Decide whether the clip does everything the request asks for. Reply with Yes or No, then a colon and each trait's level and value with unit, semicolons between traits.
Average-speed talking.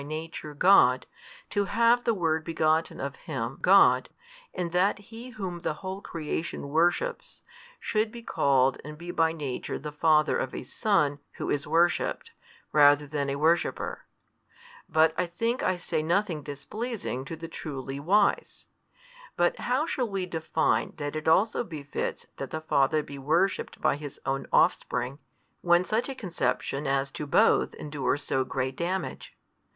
Yes: average, 155 wpm